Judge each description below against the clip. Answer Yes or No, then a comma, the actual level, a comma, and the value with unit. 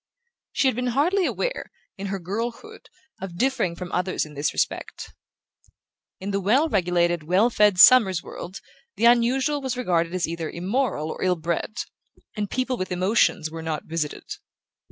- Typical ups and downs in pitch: No, wide, 6.3 semitones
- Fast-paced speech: No, average, 160 wpm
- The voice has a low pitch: No, high, 195 Hz